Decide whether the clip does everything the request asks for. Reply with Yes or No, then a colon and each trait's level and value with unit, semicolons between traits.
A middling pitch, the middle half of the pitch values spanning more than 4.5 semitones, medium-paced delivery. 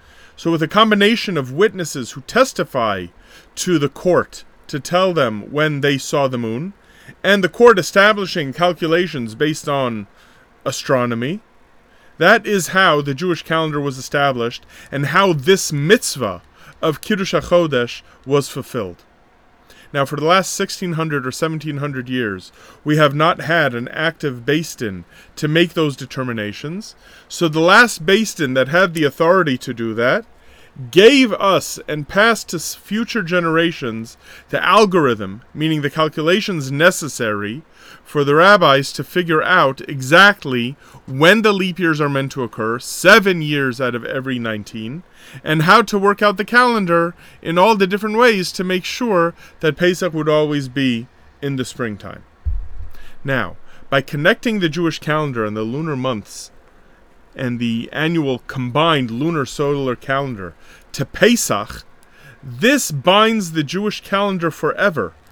Yes: medium, 155 Hz; wide, 5.6 semitones; average, 145 wpm